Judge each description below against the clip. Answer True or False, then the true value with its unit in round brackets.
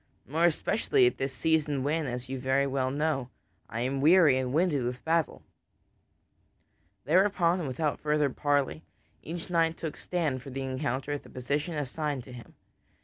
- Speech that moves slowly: False (165 wpm)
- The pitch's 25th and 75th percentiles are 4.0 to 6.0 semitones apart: False (3.6 semitones)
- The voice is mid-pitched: True (145 Hz)